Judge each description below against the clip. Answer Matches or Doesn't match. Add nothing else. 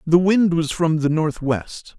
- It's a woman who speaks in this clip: Doesn't match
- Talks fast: Doesn't match